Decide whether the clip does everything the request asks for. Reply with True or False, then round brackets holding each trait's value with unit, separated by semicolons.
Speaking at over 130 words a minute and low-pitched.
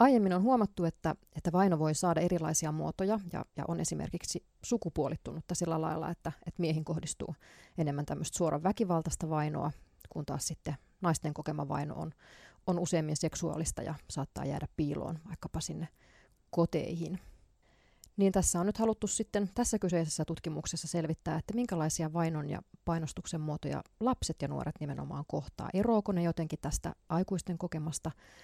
False (150 wpm; 165 Hz)